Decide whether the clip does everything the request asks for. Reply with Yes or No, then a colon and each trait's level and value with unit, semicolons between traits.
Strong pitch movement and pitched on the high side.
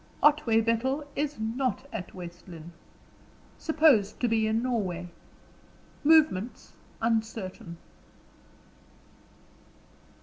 Yes: wide, 5.9 semitones; high, 225 Hz